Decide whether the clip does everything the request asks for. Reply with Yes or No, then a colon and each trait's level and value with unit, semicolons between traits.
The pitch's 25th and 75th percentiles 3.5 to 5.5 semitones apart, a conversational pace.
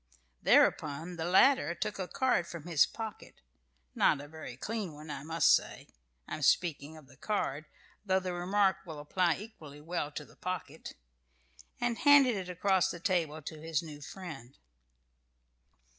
Yes: average, 4.0 semitones; average, 160 wpm